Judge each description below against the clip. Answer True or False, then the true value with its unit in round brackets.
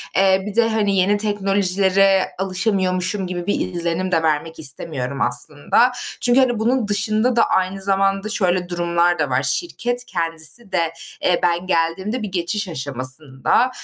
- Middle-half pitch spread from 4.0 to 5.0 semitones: False (3.6 semitones)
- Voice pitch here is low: False (185 Hz)